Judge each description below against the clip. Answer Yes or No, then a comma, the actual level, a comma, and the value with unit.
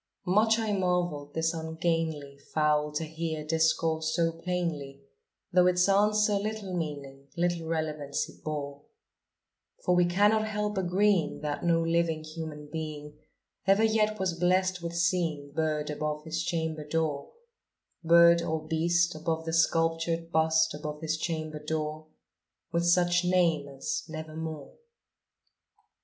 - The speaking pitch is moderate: Yes, medium, 165 Hz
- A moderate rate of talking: No, slow, 130 wpm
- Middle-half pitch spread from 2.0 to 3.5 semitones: Yes, narrow, 2.4 semitones